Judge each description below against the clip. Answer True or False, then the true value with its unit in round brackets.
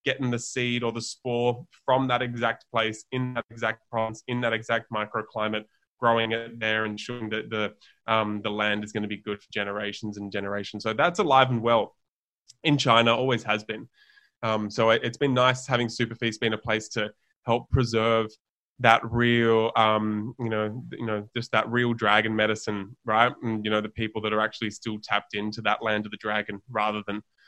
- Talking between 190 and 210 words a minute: True (200 wpm)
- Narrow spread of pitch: True (1.9 semitones)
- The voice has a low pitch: True (110 Hz)